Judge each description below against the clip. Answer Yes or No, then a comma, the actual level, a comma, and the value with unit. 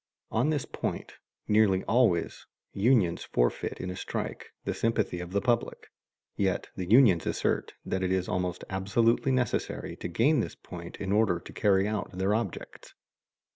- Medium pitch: No, low, 100 Hz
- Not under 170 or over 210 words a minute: No, average, 160 wpm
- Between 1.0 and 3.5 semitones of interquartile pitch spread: No, average, 4.0 semitones